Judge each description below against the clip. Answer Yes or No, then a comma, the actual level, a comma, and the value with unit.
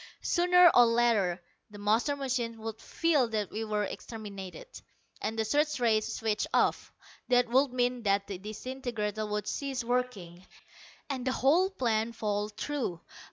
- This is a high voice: Yes, high, 230 Hz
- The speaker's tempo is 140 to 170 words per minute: Yes, average, 150 wpm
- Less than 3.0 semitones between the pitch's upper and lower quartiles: No, average, 3.5 semitones